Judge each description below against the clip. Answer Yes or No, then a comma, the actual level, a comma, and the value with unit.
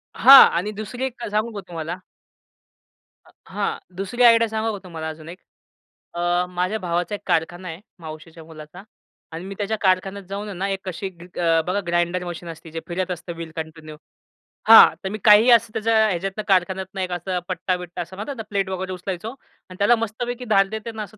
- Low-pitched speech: No, medium, 185 Hz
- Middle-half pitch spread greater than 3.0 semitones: Yes, average, 3.6 semitones